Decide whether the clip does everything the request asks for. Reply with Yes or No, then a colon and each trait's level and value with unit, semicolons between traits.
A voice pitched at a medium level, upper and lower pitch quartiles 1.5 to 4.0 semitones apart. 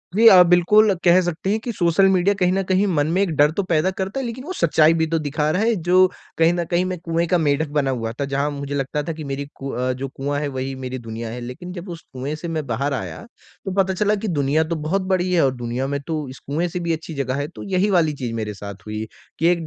No: medium, 160 Hz; average, 4.8 semitones